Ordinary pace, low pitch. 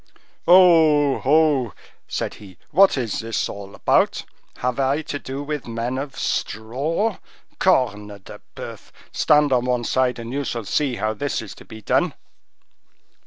Yes: average, 155 wpm; low, 130 Hz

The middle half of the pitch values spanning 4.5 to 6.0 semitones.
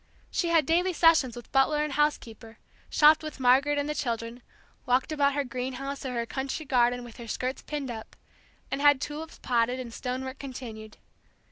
No: average, 3.3 semitones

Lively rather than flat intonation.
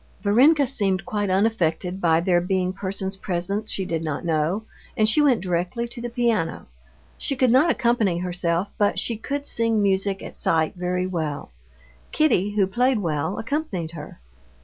No: average, 4.7 semitones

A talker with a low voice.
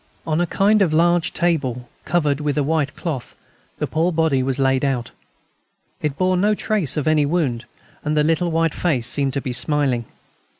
No: medium, 150 Hz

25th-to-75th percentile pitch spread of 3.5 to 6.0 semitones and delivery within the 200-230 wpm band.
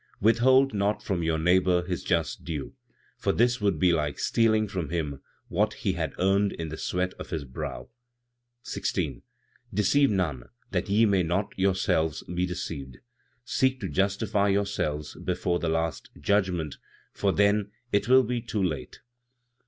No: average, 4.0 semitones; average, 155 wpm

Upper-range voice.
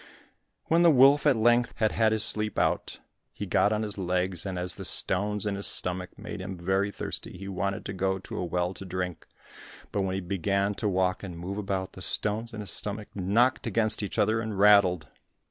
No: low, 100 Hz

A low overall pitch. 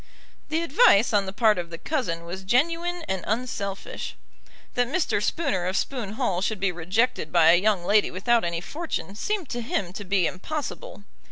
No: high, 205 Hz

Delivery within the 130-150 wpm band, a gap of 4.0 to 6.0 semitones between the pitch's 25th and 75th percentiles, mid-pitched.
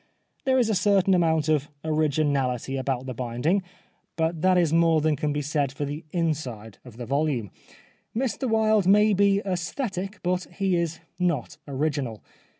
No: average, 160 wpm; average, 5.2 semitones; medium, 160 Hz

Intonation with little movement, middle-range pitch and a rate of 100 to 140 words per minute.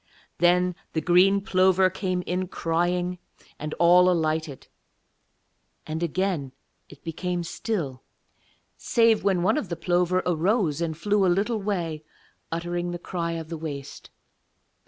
Yes: narrow, 2.2 semitones; medium, 175 Hz; slow, 135 wpm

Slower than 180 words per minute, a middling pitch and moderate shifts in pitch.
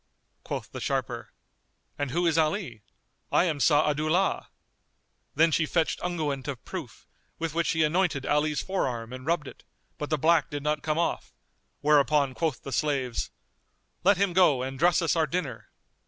Yes: average, 165 wpm; medium, 155 Hz; average, 3.0 semitones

